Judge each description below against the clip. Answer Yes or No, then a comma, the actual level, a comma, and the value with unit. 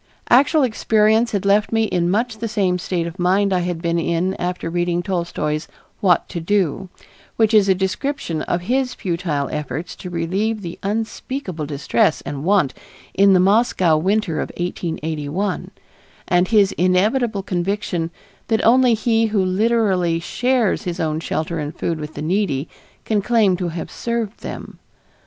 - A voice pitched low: No, medium, 185 Hz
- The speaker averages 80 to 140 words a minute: No, average, 160 wpm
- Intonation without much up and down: No, average, 4.2 semitones